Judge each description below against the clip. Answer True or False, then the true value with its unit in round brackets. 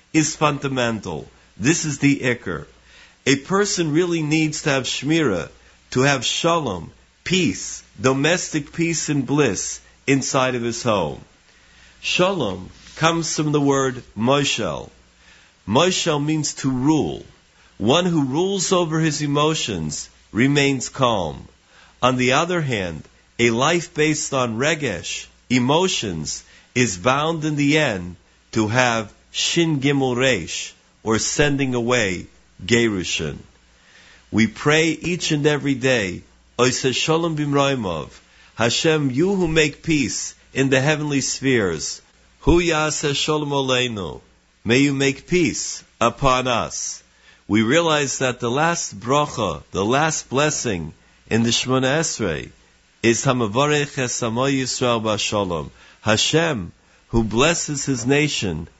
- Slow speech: True (110 wpm)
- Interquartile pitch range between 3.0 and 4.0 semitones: False (5.3 semitones)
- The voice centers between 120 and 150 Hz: True (135 Hz)